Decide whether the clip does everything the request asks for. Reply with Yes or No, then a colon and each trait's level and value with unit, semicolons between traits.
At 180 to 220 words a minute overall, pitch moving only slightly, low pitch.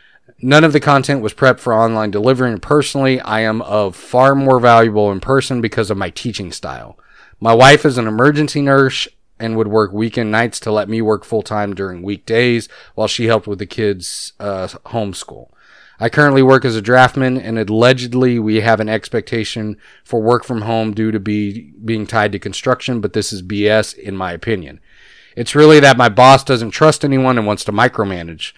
No: average, 195 wpm; average, 3.3 semitones; low, 115 Hz